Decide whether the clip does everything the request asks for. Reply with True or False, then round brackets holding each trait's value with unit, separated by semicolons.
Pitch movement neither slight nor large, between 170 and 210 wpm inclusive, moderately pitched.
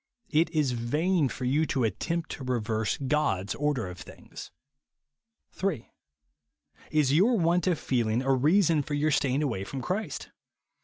False (4.6 semitones; 150 wpm; 145 Hz)